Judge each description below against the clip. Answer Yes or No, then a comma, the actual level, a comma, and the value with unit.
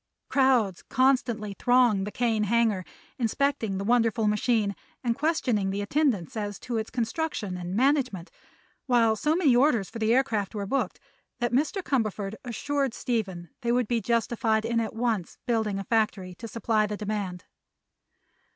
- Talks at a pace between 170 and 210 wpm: No, average, 155 wpm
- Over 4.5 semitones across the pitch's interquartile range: No, average, 3.3 semitones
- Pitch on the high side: Yes, high, 225 Hz